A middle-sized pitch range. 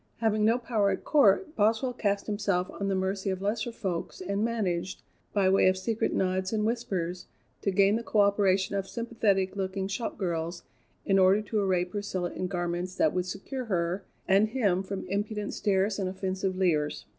No: narrow, 2.2 semitones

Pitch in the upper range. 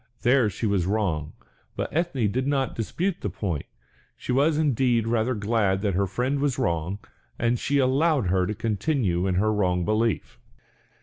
No: low, 110 Hz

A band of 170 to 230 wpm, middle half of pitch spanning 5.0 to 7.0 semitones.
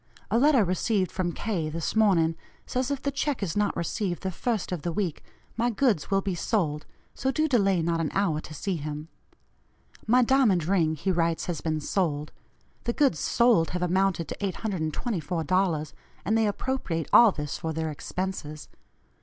Yes: average, 175 wpm; average, 5.3 semitones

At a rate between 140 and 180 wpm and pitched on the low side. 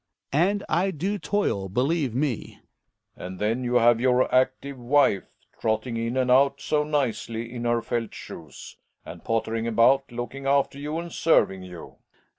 Yes: average, 165 wpm; low, 125 Hz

